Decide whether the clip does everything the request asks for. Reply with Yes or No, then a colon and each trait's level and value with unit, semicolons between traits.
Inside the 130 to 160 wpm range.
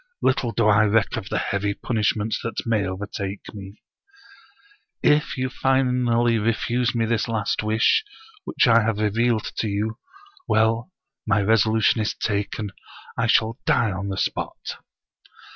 Yes: average, 150 wpm